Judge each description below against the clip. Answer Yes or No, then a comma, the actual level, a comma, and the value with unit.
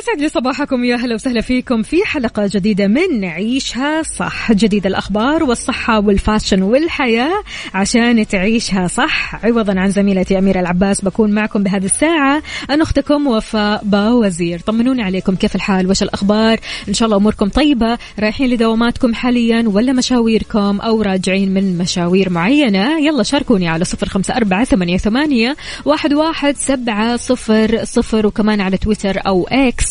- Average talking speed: Yes, average, 145 wpm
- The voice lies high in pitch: Yes, high, 220 Hz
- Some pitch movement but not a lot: Yes, average, 4.2 semitones